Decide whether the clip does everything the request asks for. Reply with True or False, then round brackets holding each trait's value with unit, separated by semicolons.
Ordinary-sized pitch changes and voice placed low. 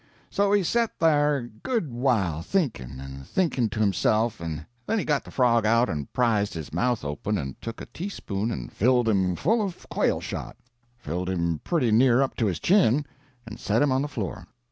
False (7.8 semitones; 115 Hz)